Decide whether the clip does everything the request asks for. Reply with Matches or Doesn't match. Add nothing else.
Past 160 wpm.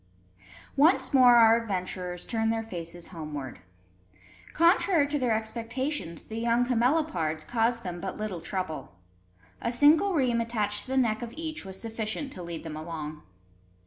Doesn't match